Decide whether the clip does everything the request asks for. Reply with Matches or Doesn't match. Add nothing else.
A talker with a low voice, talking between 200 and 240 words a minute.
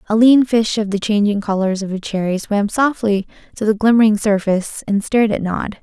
Doesn't match